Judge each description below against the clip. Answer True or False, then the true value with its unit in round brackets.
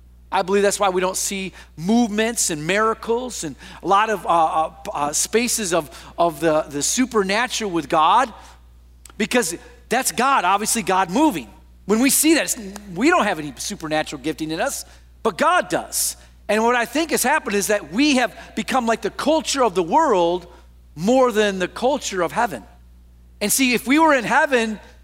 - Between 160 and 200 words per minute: True (180 wpm)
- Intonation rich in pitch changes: True (7.0 semitones)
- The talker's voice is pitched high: True (205 Hz)